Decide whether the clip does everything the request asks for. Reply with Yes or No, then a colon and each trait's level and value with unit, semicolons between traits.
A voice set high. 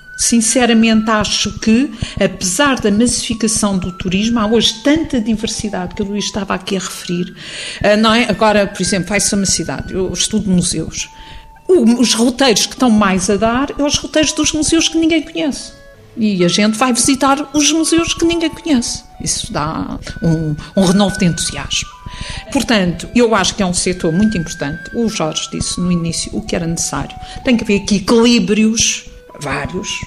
Yes: high, 215 Hz